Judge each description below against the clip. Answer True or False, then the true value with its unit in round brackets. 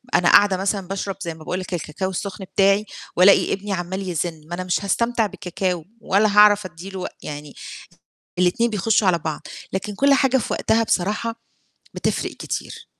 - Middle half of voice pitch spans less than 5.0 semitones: True (2.8 semitones)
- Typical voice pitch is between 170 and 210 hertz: True (190 Hz)